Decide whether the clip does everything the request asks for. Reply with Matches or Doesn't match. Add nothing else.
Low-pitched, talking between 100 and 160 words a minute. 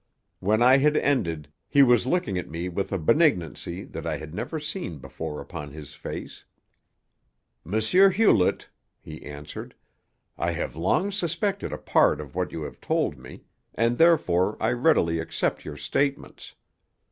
Matches